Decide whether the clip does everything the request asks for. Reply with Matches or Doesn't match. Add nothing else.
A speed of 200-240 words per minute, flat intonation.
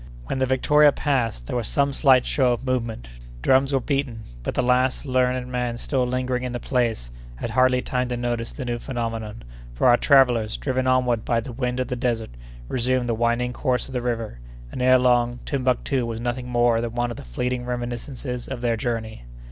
Matches